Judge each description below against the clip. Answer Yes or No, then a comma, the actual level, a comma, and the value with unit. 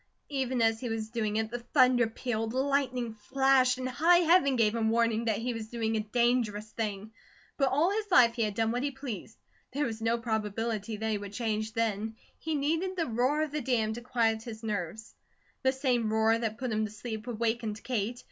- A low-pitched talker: No, high, 230 Hz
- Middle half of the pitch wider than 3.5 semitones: No, average, 2.7 semitones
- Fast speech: Yes, fast, 210 wpm